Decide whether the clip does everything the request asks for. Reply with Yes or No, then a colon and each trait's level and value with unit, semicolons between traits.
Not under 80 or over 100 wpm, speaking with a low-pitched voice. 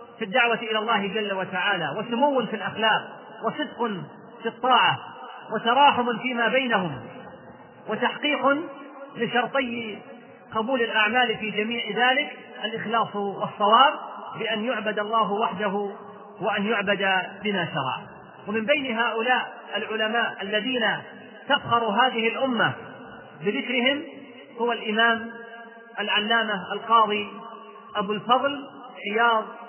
No: average, 95 wpm; high, 225 Hz